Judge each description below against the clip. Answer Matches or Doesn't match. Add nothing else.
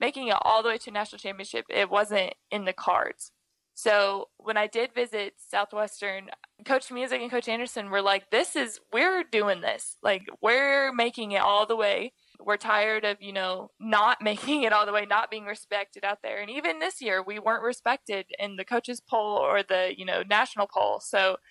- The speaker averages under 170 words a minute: Doesn't match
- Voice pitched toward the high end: Matches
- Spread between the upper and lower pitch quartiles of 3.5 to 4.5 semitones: Doesn't match